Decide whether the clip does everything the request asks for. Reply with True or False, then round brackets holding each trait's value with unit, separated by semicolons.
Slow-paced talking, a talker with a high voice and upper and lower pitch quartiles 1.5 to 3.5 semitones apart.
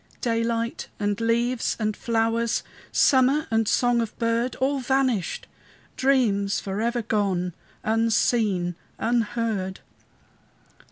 True (95 wpm; 230 Hz; 2.5 semitones)